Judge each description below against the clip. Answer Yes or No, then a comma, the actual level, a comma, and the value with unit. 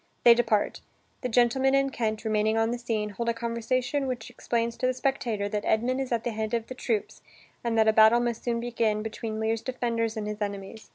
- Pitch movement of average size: No, narrow, 1.8 semitones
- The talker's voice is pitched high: Yes, high, 230 Hz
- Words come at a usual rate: No, fast, 220 wpm